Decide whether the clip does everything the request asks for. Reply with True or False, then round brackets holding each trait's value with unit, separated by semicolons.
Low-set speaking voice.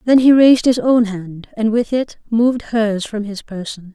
False (220 Hz)